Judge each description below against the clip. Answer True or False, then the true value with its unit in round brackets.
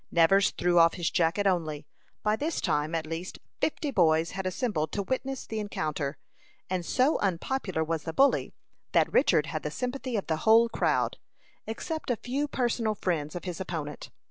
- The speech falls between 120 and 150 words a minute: False (175 wpm)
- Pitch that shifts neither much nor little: False (6.5 semitones)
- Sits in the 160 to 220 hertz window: True (185 Hz)